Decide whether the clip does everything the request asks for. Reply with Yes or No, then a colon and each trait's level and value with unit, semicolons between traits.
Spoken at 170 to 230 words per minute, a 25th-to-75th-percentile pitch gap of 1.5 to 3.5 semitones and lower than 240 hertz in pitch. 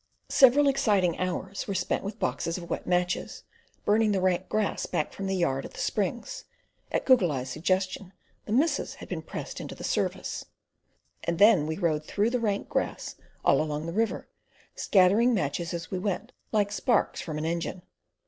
No: average, 175 wpm; average, 3.9 semitones; medium, 185 Hz